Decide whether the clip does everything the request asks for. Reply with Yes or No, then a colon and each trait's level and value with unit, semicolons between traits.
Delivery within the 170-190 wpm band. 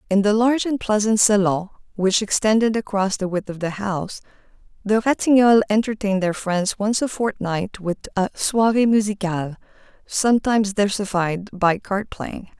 No: average, 150 wpm